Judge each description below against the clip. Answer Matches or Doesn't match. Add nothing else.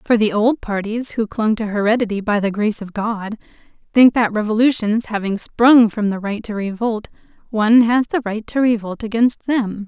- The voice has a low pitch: Doesn't match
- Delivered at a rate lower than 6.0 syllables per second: Matches